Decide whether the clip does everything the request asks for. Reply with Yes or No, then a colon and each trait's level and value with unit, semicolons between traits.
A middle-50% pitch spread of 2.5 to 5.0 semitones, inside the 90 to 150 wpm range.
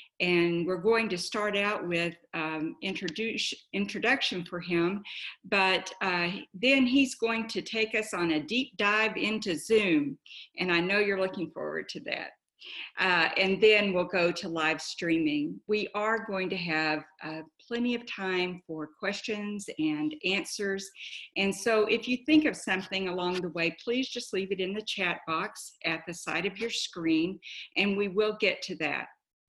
No: average, 4.0 semitones; average, 175 wpm